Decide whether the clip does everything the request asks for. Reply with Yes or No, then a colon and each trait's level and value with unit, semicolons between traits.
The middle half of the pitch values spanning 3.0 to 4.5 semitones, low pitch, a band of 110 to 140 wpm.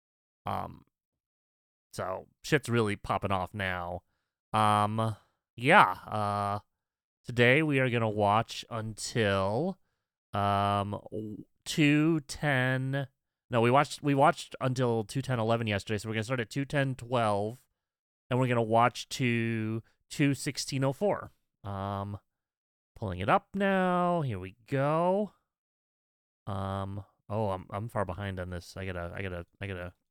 No: average, 5.2 semitones; low, 110 Hz; slow, 135 wpm